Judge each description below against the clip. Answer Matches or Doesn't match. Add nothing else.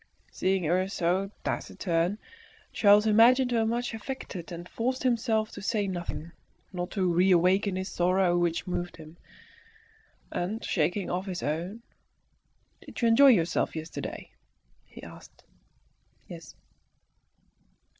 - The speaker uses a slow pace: Matches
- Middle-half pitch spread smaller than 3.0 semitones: Doesn't match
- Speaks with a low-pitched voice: Doesn't match